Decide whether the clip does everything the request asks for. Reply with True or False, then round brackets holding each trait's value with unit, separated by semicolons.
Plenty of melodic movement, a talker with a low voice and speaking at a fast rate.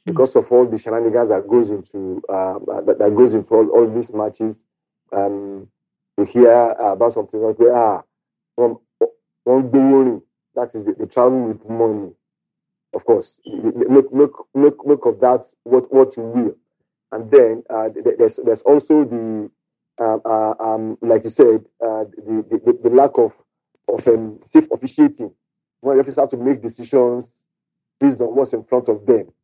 False (6.7 semitones; 125 Hz; 155 wpm)